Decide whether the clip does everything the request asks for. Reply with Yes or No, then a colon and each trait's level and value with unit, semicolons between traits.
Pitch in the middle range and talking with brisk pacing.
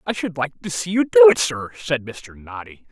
Yes: medium, 160 Hz; fast, 245 wpm